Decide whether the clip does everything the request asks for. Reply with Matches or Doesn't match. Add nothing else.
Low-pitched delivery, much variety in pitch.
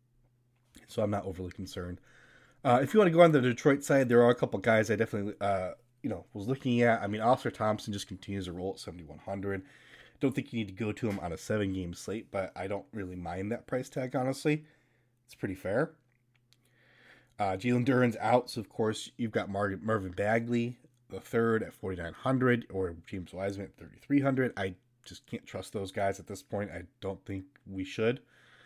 Doesn't match